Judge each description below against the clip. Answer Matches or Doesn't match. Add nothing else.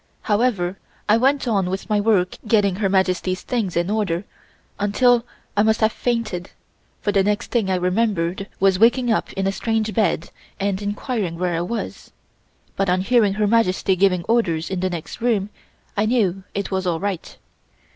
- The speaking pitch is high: Matches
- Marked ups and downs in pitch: Doesn't match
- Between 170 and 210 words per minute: Matches